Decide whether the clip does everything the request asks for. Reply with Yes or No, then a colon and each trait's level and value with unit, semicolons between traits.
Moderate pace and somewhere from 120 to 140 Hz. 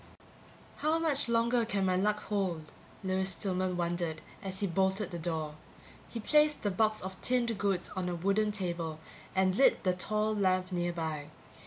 No: average, 165 wpm; high, 190 Hz